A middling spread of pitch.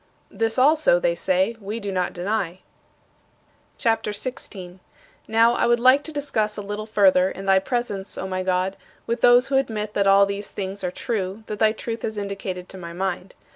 Yes: average, 3.6 semitones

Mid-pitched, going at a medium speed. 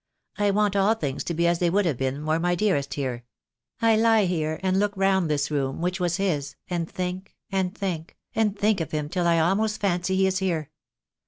No: medium, 180 Hz; fast, 220 wpm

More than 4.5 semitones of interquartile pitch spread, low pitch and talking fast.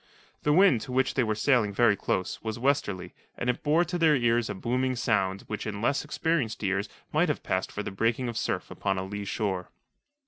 Yes: average, 5.2 semitones; low, 115 Hz; fast, 215 wpm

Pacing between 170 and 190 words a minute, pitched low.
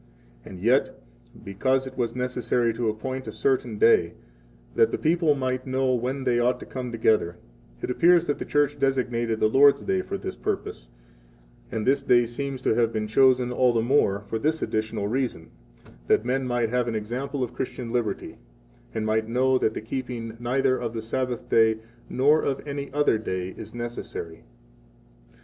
Yes: average, 180 wpm; low, 125 Hz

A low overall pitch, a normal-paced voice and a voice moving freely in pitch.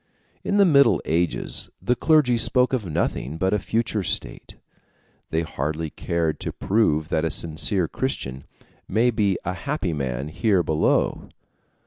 Yes: very low, 90 Hz; average, 145 wpm; wide, 7.0 semitones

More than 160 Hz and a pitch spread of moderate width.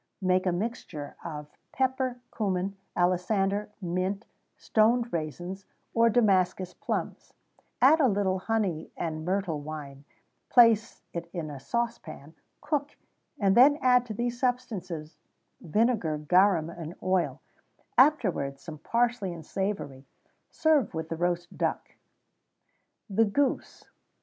No: high, 190 Hz; wide, 5.7 semitones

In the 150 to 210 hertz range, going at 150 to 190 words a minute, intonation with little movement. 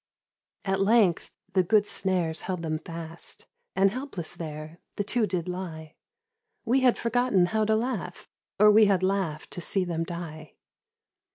No: medium, 185 Hz; average, 155 wpm; average, 4.2 semitones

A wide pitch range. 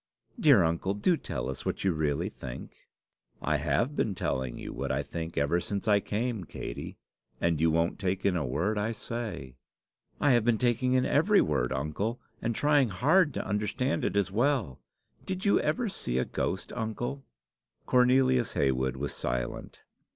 Yes: wide, 8.1 semitones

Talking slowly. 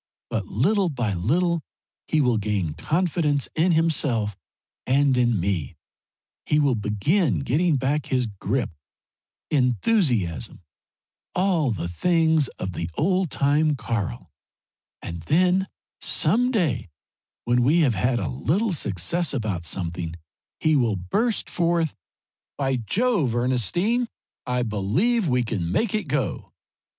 Yes: slow, 125 wpm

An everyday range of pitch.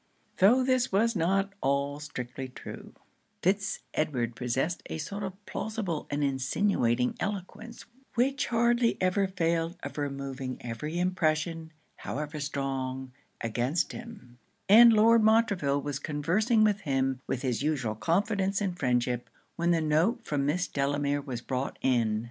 No: wide, 6.9 semitones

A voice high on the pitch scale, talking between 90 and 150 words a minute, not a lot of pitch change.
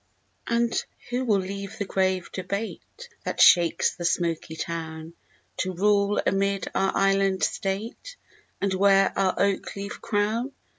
Yes: high, 195 Hz; slow, 135 wpm; narrow, 1.6 semitones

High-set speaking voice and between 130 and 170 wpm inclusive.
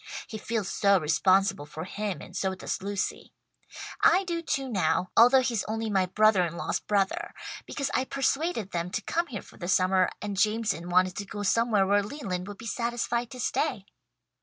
No: high, 205 Hz; average, 185 wpm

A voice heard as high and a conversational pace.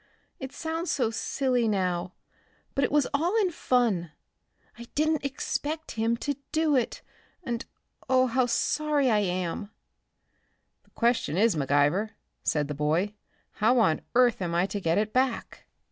Yes: high, 235 Hz; average, 150 wpm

